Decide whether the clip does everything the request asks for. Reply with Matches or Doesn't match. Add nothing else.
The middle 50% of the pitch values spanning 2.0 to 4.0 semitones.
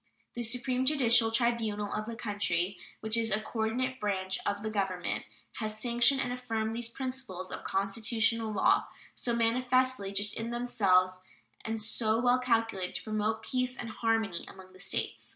Matches